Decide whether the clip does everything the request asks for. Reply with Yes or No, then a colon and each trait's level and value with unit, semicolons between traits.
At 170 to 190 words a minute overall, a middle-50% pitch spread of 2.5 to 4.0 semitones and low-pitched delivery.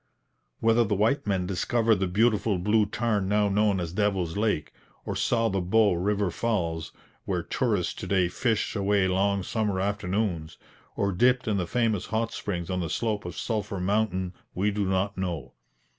Yes: average, 175 wpm; average, 2.9 semitones; low, 100 Hz